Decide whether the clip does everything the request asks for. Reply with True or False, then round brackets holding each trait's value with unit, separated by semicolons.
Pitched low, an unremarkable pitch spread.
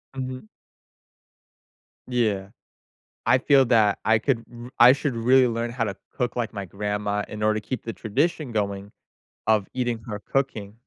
True (115 Hz; 3.5 semitones)